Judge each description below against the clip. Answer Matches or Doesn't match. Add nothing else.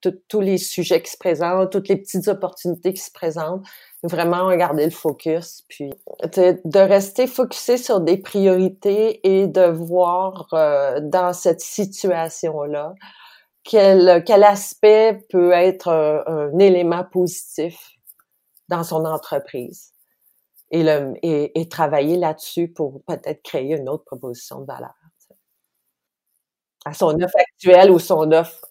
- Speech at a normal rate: Doesn't match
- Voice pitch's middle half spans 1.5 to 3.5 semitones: Matches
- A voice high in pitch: Doesn't match